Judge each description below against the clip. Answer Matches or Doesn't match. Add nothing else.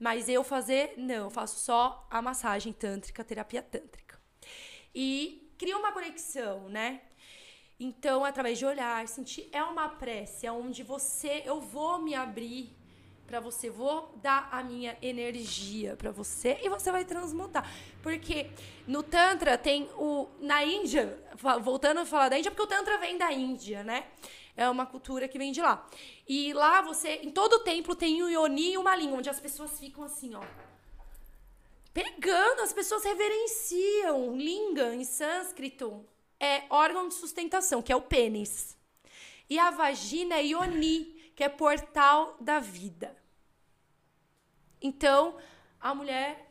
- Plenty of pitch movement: Doesn't match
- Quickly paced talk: Doesn't match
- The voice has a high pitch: Matches